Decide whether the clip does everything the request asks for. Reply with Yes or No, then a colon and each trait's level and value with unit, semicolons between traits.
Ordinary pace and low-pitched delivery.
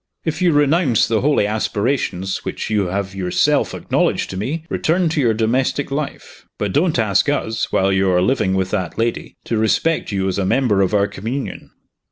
Yes: average, 190 wpm; low, 110 Hz